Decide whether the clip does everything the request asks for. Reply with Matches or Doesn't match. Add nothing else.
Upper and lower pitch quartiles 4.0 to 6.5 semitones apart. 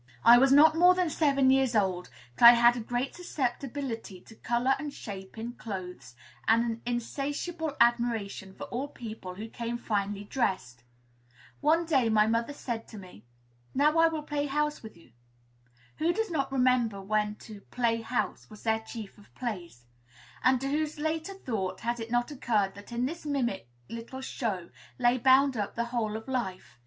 Matches